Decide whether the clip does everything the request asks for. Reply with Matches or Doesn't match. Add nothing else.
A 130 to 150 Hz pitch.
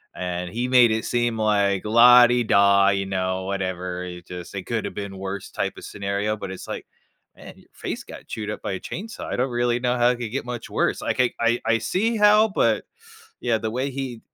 Doesn't match